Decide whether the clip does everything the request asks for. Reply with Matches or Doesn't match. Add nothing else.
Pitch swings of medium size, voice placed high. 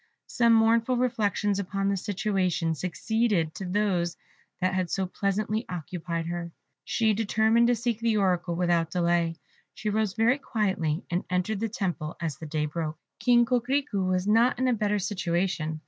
Matches